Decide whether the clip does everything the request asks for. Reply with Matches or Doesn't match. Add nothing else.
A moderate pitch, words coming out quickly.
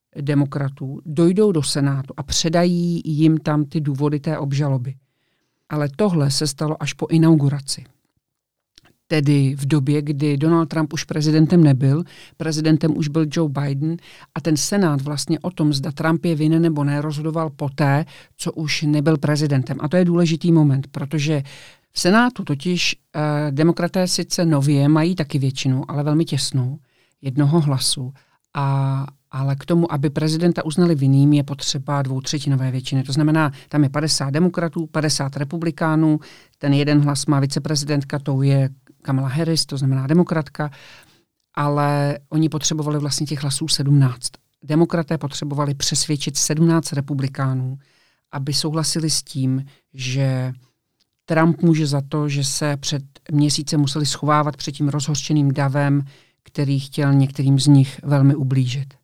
Doesn't match